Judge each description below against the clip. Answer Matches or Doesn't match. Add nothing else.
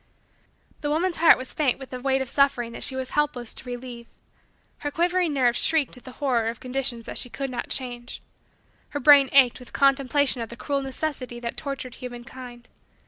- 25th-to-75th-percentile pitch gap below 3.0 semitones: Matches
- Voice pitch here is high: Matches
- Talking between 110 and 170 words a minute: Doesn't match